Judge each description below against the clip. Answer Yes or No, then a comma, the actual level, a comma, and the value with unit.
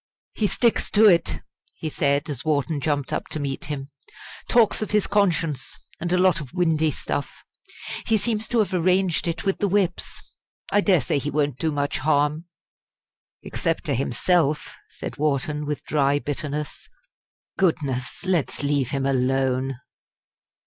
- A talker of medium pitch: Yes, medium, 150 Hz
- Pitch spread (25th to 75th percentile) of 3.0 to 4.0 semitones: No, average, 4.4 semitones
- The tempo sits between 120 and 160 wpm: Yes, average, 155 wpm